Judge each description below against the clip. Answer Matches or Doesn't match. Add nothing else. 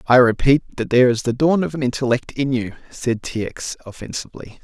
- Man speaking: Matches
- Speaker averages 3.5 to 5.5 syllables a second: Doesn't match